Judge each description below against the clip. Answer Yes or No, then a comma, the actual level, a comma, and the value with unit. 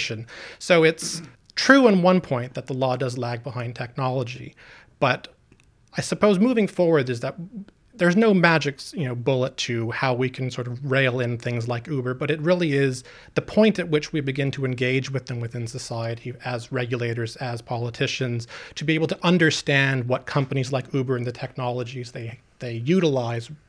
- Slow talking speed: No, average, 180 wpm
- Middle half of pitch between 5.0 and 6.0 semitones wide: No, average, 4.2 semitones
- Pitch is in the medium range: No, low, 130 Hz